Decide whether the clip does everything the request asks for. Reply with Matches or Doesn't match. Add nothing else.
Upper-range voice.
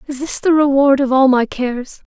Matches